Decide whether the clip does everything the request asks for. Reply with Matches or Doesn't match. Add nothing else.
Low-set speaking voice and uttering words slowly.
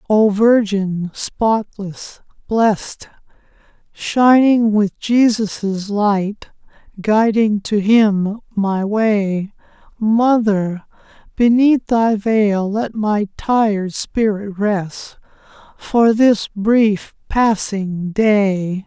Doesn't match